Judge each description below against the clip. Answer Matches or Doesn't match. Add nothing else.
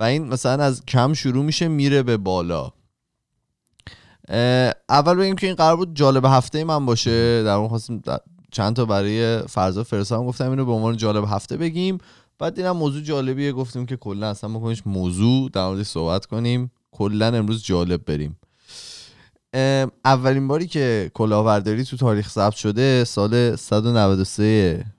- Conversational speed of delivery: Doesn't match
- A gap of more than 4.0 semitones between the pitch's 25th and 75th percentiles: Matches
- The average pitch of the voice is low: Matches